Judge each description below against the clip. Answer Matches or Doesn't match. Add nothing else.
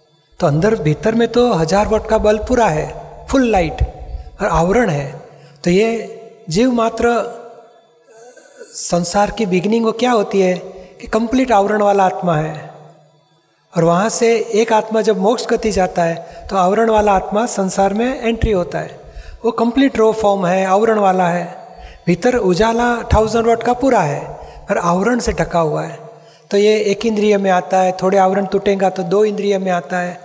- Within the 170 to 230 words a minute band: Matches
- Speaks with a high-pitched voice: Matches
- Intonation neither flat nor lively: Matches